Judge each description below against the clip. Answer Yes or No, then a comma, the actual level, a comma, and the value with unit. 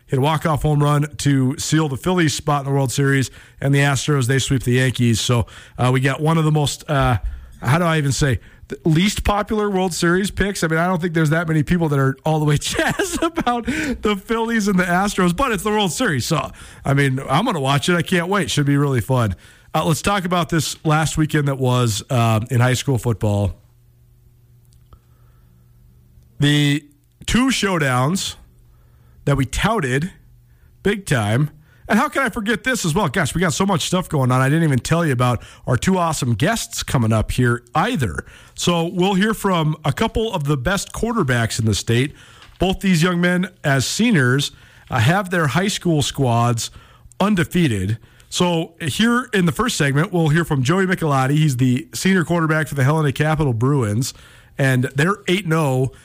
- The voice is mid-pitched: Yes, medium, 145 Hz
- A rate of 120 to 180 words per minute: No, average, 195 wpm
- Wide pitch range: Yes, wide, 6.2 semitones